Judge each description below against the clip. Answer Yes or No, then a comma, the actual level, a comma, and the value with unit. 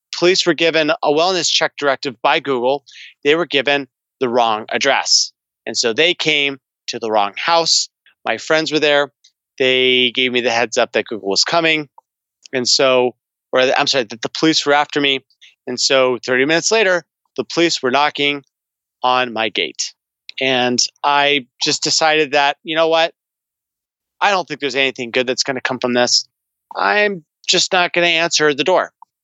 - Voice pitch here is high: No, medium, 140 Hz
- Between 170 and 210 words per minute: Yes, average, 180 wpm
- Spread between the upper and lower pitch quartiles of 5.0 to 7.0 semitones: No, average, 3.9 semitones